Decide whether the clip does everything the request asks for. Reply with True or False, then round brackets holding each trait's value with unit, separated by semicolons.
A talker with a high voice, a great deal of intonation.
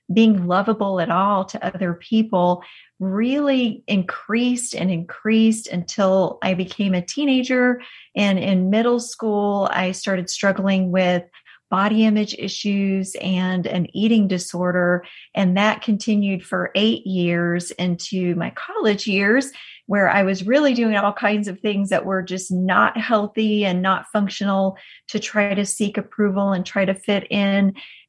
False (200 Hz; 2.5 semitones)